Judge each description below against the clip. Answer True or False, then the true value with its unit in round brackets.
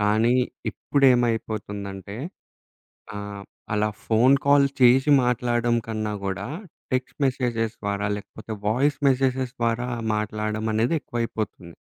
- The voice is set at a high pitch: False (115 Hz)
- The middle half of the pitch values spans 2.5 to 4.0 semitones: True (2.9 semitones)